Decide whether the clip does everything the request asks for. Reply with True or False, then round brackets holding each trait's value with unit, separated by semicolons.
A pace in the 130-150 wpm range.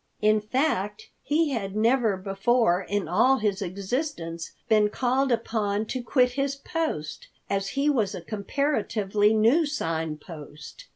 True (135 wpm)